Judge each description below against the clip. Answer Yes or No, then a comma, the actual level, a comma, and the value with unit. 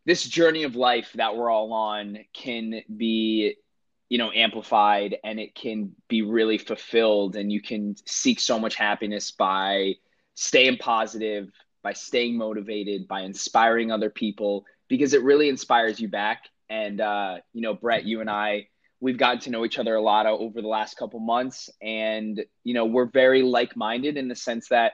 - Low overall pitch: Yes, low, 110 Hz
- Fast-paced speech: No, average, 175 wpm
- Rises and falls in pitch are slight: Yes, narrow, 2.3 semitones